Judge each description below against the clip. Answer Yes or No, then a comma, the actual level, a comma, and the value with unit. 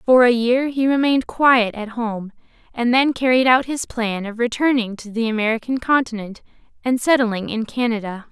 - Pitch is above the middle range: Yes, high, 240 Hz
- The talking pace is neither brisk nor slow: Yes, average, 175 wpm